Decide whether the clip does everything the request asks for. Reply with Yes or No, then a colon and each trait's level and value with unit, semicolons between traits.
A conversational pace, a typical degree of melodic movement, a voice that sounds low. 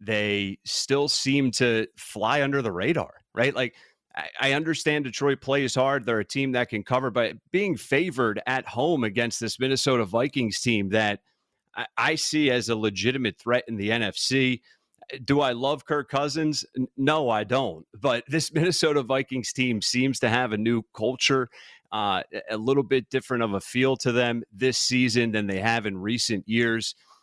Yes: average, 170 wpm; average, 3.2 semitones; low, 125 Hz